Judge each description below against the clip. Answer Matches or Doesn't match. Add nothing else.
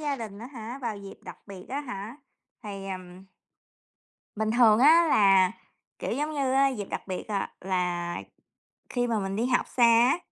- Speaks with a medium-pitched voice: Doesn't match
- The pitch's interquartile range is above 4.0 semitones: Matches